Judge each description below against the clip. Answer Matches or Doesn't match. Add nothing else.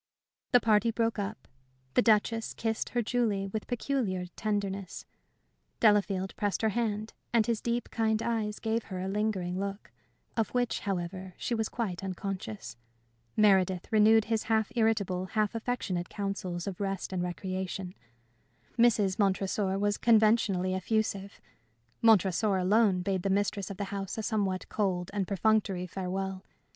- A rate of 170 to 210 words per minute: Doesn't match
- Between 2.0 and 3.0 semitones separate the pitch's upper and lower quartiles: Matches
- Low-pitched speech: Doesn't match